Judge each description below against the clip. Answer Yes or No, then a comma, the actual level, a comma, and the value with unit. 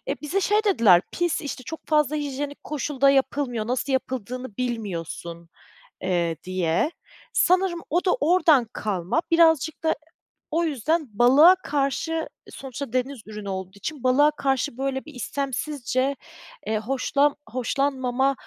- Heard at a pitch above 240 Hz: Yes, very high, 270 Hz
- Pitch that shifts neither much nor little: Yes, average, 4.4 semitones